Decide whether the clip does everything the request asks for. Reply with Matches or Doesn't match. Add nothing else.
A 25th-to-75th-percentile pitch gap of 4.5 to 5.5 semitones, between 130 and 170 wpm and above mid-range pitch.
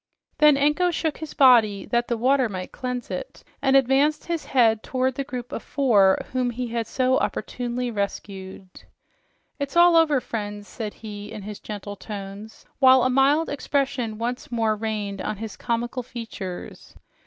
Doesn't match